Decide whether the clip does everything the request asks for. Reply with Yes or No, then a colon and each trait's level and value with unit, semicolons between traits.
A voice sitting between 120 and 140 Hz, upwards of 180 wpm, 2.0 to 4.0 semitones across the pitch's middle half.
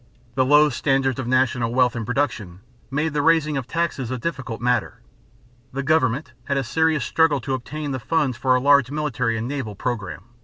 Yes: low, 135 Hz; average, 190 wpm; average, 3.4 semitones